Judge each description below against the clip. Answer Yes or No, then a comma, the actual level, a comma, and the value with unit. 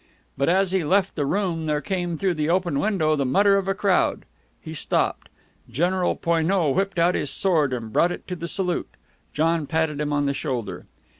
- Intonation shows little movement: No, average, 4.1 semitones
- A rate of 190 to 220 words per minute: Yes, average, 200 wpm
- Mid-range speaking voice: Yes, medium, 170 Hz